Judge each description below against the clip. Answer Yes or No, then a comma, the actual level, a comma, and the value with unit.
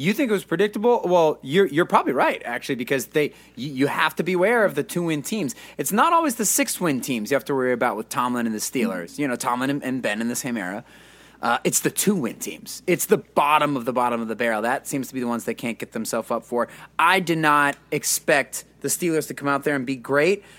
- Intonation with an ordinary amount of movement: No, wide, 6.4 semitones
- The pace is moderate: No, fast, 255 wpm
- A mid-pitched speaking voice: Yes, medium, 145 Hz